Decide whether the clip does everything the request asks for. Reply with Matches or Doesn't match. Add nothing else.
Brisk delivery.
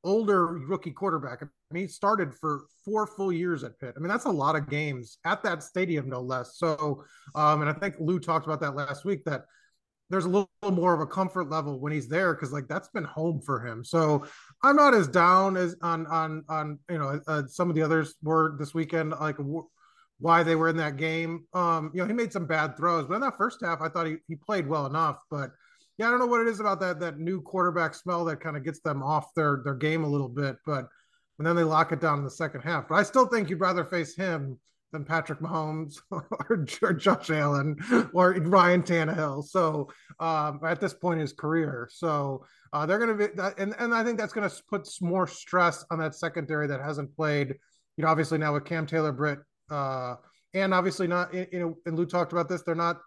Matches